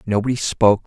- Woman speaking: No, male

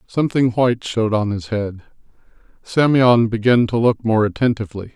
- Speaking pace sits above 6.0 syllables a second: No, 5.6 syllables/s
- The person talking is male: Yes, male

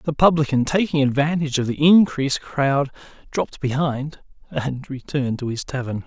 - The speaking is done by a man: Yes, male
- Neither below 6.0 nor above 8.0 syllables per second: No, 5.2 syllables/s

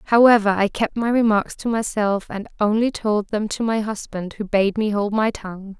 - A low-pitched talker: No, high, 210 Hz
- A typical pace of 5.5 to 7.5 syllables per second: No, 5.0 syllables/s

